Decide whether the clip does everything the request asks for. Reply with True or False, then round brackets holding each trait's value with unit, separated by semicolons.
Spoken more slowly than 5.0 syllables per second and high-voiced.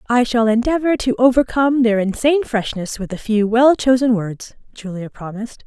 False (5.3 syllables/s; 235 Hz)